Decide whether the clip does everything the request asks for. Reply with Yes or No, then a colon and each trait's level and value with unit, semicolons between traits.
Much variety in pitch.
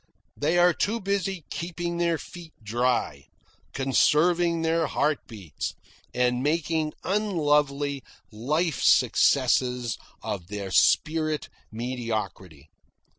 Yes: wide, 5.8 semitones